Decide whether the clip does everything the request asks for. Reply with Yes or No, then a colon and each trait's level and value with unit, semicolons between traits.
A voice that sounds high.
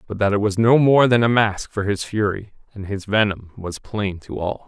No: low, 105 Hz